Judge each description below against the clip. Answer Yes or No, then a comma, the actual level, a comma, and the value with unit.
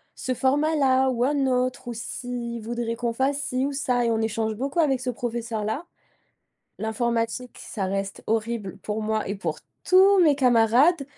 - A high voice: Yes, high, 240 Hz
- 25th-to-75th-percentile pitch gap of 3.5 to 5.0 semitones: No, average, 3.1 semitones